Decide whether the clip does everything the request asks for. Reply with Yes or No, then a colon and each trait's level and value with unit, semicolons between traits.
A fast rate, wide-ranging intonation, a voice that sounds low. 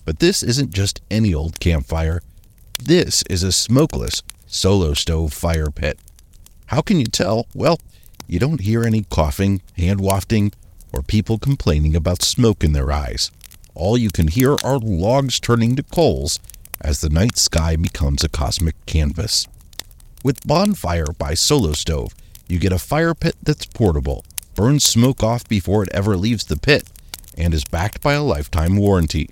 No: average, 165 wpm; wide, 5.9 semitones; very low, 95 Hz